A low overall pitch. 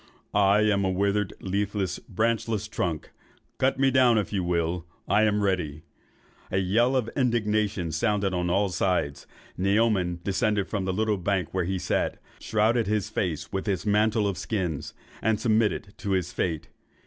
Yes: low, 100 Hz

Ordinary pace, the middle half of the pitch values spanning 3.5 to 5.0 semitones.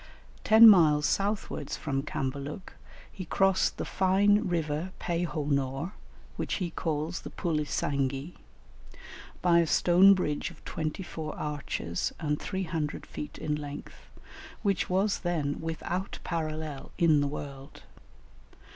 No: slow, 125 wpm; average, 3.9 semitones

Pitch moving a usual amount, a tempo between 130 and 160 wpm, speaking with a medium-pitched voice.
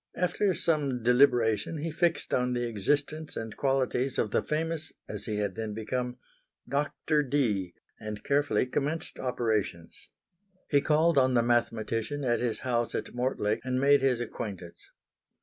No: average, 4.4 semitones; average, 150 wpm; low, 125 Hz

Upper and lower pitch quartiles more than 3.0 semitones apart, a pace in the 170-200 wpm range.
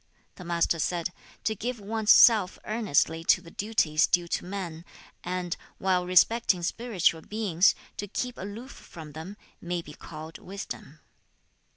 No: average, 3.9 semitones; average, 145 wpm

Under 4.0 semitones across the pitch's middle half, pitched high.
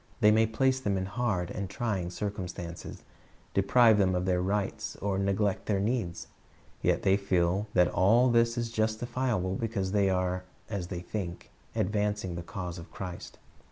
No: average, 3.2 semitones; low, 100 Hz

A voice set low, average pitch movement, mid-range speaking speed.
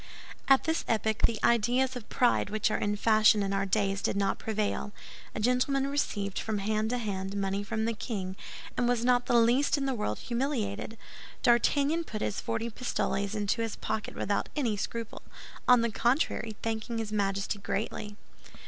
No: high, 220 Hz; average, 3.1 semitones; average, 175 wpm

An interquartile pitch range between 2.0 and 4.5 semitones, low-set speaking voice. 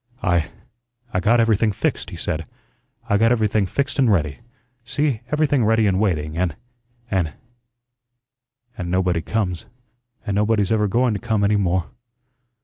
Yes: average, 3.8 semitones; low, 105 Hz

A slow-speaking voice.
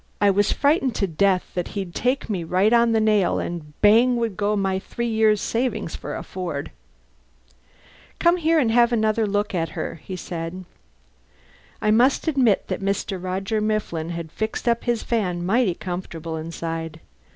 No: average, 165 wpm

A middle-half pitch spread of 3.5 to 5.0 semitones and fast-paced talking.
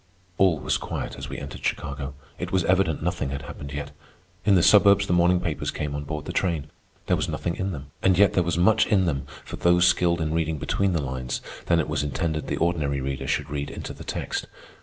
Yes: average, 3.8 semitones; fast, 230 wpm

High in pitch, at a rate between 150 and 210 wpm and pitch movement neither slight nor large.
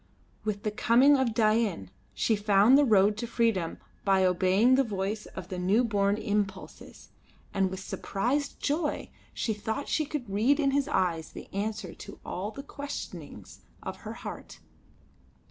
Yes: high, 215 Hz; average, 160 wpm; average, 4.3 semitones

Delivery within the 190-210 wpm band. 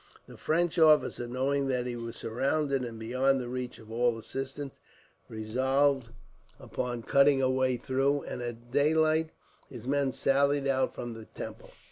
No: average, 155 wpm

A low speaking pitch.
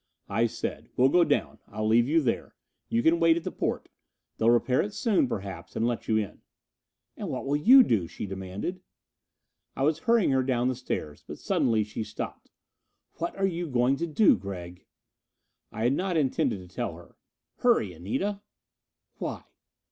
Yes: low, 125 Hz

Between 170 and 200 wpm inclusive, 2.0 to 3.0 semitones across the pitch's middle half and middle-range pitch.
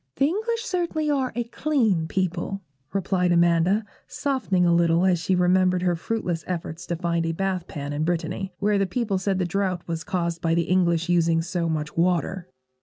Yes: average, 185 wpm; average, 2.7 semitones; medium, 180 Hz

